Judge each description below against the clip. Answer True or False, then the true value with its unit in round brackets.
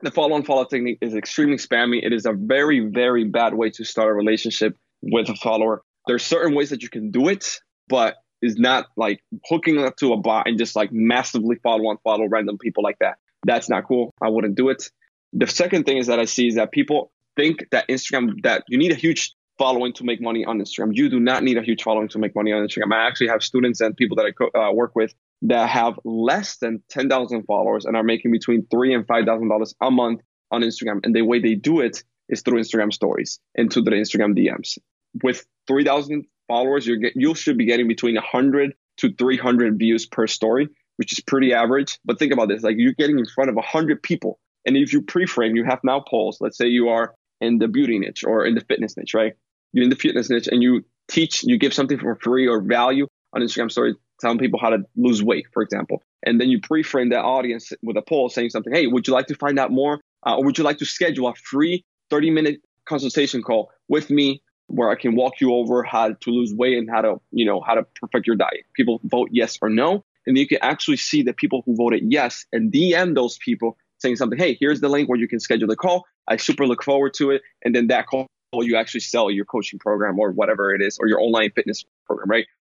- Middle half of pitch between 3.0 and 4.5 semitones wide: True (3.5 semitones)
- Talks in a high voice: False (120 Hz)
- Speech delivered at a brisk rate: True (235 wpm)